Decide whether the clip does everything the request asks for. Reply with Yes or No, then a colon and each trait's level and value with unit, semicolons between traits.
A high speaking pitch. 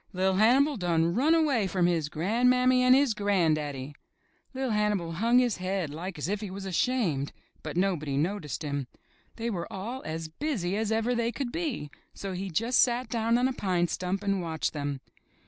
Yes: high, 195 Hz